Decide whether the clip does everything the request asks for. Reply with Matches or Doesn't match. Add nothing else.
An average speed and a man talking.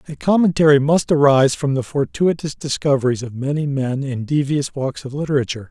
Matches